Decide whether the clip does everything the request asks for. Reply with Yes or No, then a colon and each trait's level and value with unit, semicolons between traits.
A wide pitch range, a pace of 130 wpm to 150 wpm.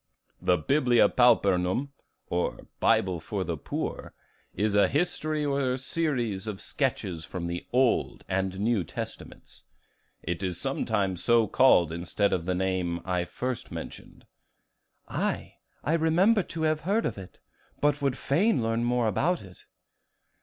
Yes: wide, 7.3 semitones; average, 140 wpm